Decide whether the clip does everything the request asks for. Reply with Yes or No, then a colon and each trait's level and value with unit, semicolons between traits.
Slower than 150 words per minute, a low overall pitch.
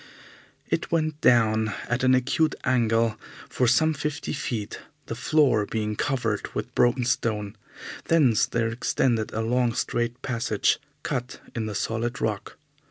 Yes: average, 140 wpm; low, 120 Hz